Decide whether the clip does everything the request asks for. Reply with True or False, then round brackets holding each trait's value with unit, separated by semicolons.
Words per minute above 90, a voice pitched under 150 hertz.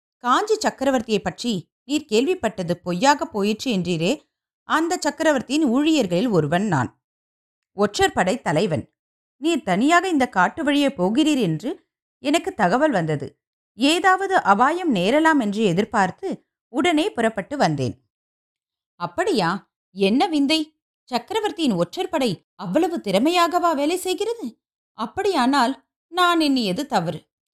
False (105 wpm; 265 Hz)